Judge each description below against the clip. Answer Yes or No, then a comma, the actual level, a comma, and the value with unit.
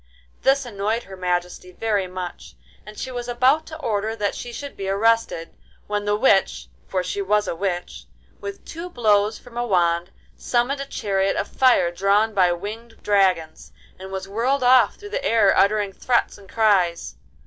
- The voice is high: Yes, high, 205 Hz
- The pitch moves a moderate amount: Yes, average, 4.0 semitones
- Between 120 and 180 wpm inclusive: Yes, average, 170 wpm